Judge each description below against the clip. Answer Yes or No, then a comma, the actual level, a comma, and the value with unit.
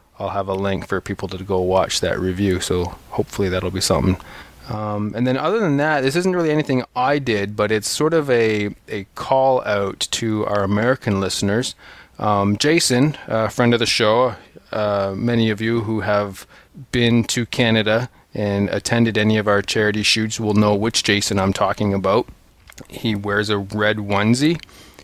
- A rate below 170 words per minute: No, average, 180 wpm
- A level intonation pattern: No, average, 3.3 semitones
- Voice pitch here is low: Yes, low, 105 Hz